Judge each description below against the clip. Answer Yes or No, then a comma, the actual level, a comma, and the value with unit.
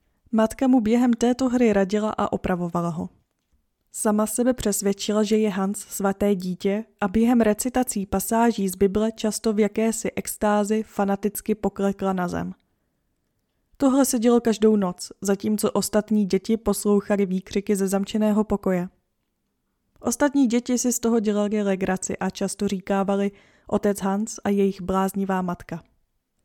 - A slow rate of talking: No, average, 135 wpm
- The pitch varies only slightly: Yes, narrow, 2.1 semitones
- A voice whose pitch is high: Yes, high, 205 Hz